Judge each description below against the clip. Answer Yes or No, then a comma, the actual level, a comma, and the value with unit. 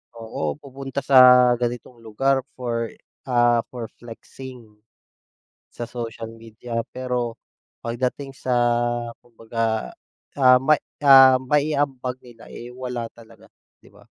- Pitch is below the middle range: Yes, low, 125 Hz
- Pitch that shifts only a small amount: Yes, narrow, 2.0 semitones